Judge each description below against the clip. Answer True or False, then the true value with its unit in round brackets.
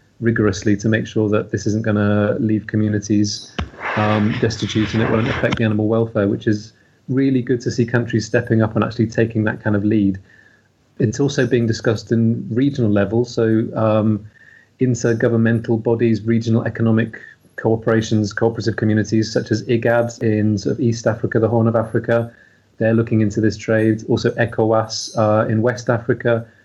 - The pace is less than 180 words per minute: True (170 wpm)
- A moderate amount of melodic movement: False (1.5 semitones)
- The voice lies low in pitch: True (110 Hz)